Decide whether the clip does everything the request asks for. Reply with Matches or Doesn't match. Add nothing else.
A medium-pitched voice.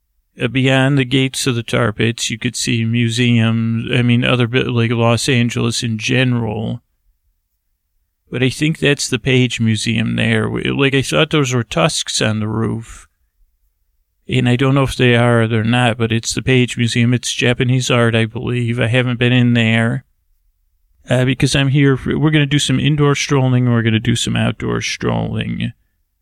Doesn't match